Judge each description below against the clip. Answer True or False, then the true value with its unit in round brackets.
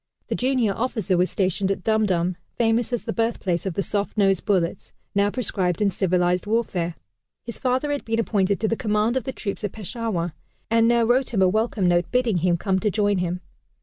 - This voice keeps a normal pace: False (210 wpm)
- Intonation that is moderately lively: True (3.9 semitones)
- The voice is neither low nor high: False (205 Hz)